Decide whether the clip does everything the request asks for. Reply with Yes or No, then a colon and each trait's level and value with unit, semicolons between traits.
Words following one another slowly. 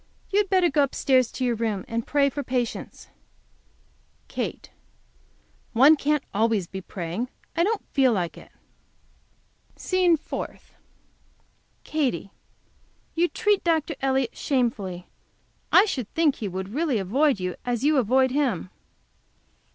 Yes: slow, 130 wpm